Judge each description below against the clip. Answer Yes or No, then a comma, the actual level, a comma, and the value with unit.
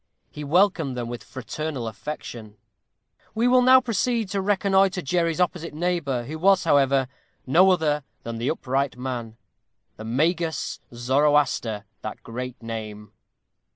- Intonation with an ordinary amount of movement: No, wide, 6.8 semitones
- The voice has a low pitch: No, medium, 145 Hz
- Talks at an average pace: No, slow, 130 wpm